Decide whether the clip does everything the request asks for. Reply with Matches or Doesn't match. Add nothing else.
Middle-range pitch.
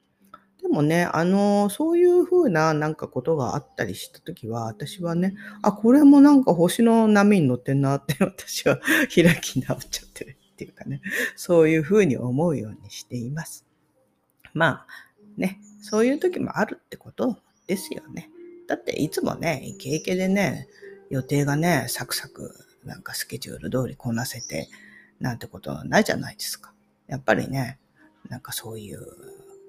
Matches